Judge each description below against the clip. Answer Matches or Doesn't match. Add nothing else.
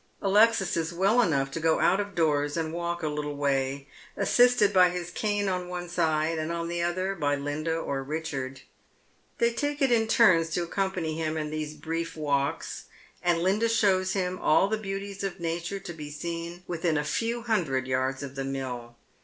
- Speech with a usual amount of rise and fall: Matches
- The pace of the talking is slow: Doesn't match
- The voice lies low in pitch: Doesn't match